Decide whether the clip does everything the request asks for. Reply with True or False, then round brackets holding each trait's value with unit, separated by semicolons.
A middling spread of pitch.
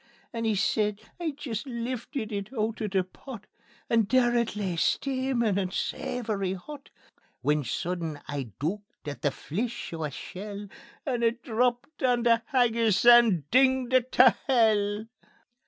True (4.0 semitones)